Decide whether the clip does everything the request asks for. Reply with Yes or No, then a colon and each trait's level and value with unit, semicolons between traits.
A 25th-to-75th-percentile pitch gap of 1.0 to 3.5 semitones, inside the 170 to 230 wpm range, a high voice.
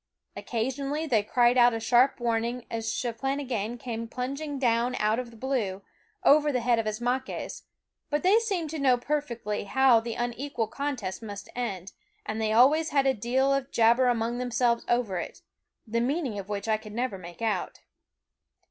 Yes: average, 3.0 semitones; average, 175 wpm; high, 240 Hz